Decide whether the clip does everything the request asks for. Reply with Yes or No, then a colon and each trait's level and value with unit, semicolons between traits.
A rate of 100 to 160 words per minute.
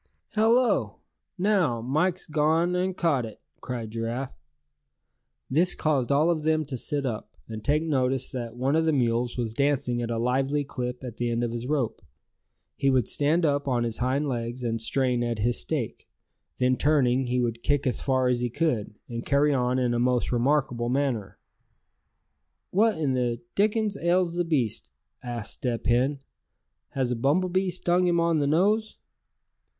No: average, 175 wpm